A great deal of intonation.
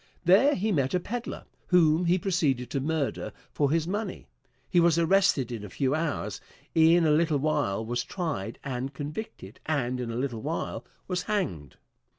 Yes: wide, 5.8 semitones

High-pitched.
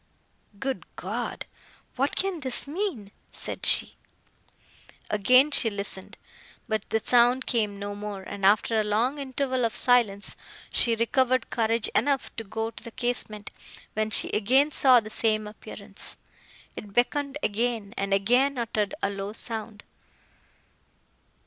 Yes: high, 225 Hz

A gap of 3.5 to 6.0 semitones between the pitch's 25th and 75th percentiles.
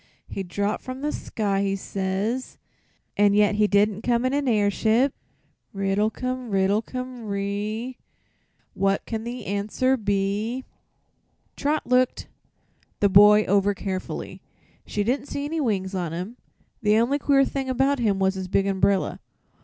Yes: average, 4.3 semitones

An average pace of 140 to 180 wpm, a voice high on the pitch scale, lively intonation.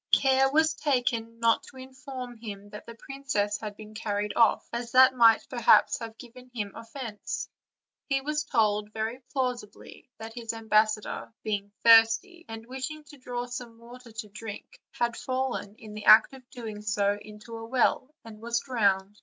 No: average, 170 wpm; high, 230 Hz; average, 3.1 semitones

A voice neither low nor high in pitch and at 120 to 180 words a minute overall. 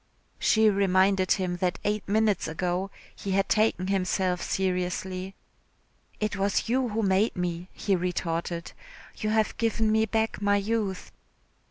No: high, 195 Hz; average, 140 wpm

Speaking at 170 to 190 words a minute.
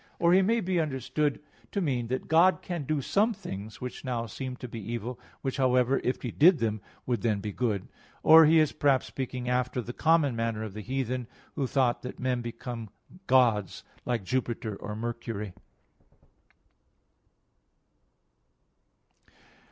No: average, 155 wpm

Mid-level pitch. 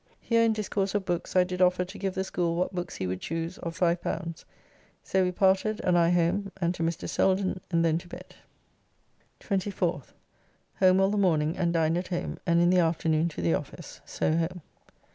Yes: medium, 175 Hz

